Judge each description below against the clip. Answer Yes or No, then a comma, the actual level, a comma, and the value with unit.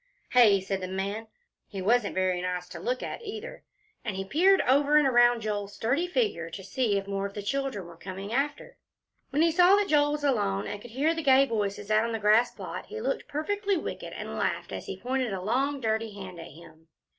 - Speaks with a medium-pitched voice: No, high, 230 Hz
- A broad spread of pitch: Yes, wide, 6.7 semitones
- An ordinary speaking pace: No, fast, 230 wpm